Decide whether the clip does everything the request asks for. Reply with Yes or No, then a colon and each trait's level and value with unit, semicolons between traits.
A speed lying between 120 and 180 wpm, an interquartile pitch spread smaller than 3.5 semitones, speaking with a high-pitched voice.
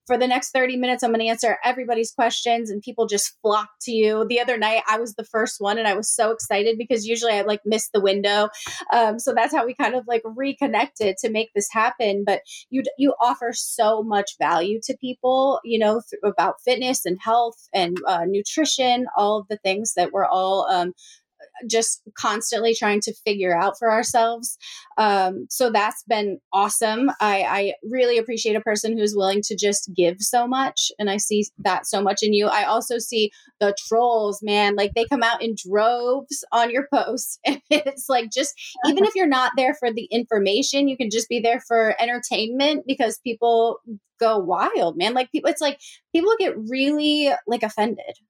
No: average, 195 wpm; average, 3.1 semitones; high, 230 Hz